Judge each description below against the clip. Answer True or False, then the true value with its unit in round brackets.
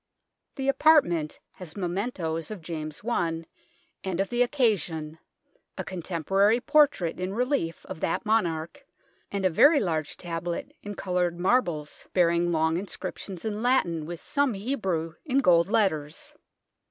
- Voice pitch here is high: False (180 Hz)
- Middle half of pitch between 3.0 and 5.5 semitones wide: True (5.1 semitones)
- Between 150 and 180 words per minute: False (140 wpm)